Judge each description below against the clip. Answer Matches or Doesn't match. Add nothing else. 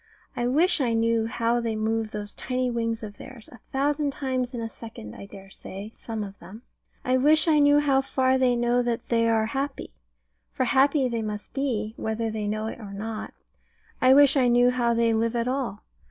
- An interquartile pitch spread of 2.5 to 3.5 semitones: Matches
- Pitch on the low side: Doesn't match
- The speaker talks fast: Matches